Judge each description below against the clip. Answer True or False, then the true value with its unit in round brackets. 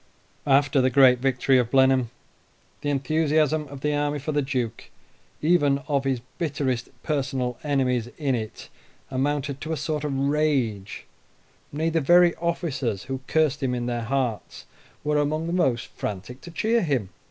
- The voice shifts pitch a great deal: False (3.0 semitones)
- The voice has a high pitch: False (140 Hz)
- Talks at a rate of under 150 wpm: False (160 wpm)